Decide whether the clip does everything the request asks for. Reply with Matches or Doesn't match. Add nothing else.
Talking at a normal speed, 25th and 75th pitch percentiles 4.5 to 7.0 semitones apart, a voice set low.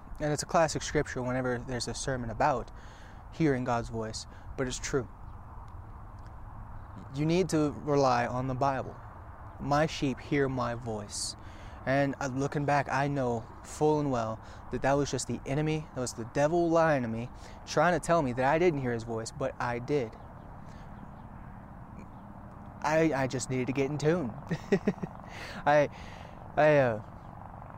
Matches